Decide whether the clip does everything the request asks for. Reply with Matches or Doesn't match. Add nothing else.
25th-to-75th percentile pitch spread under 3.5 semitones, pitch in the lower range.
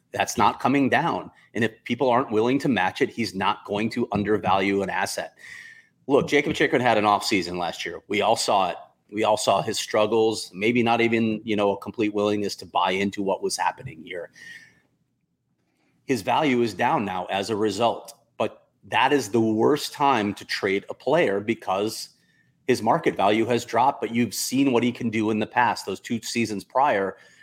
Matches